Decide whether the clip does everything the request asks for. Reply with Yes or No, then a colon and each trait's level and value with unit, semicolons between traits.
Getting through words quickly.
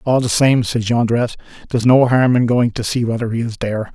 Yes: fast, 245 wpm